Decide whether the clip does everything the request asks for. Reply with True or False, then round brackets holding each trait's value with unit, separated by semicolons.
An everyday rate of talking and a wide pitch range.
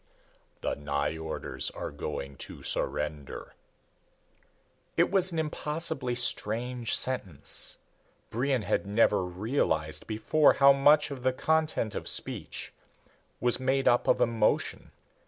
False (115 wpm; 7.3 semitones)